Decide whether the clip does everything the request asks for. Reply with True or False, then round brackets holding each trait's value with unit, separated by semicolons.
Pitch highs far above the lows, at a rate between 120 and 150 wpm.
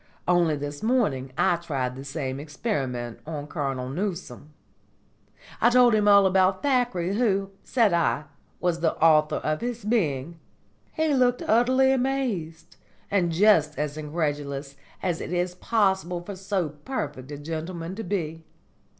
True (5.8 semitones; 140 wpm)